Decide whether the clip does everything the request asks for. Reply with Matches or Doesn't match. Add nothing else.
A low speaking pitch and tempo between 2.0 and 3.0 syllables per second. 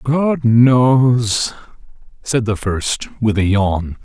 Matches